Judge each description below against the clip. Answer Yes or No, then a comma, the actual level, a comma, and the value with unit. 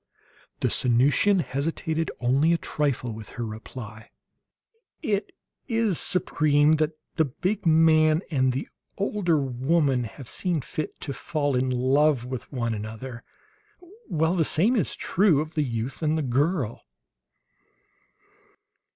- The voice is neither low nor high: Yes, medium, 145 Hz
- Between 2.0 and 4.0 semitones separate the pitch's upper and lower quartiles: No, average, 4.4 semitones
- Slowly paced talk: Yes, slow, 130 wpm